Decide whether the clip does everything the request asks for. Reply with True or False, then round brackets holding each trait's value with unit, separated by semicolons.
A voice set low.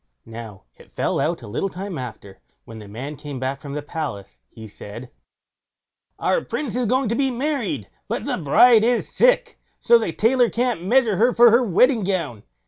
False (185 Hz)